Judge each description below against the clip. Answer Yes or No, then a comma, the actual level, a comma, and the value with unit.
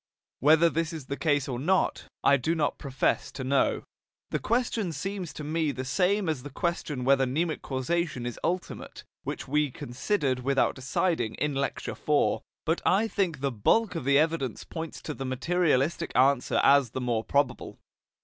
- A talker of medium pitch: Yes, medium, 145 Hz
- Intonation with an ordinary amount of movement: Yes, average, 4.4 semitones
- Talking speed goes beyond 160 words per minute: Yes, average, 175 wpm